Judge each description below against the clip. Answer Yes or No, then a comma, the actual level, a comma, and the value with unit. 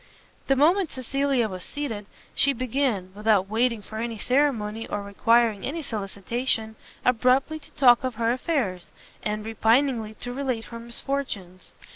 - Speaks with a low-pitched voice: No, high, 235 Hz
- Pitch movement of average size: Yes, average, 4.0 semitones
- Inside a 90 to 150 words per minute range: Yes, average, 140 wpm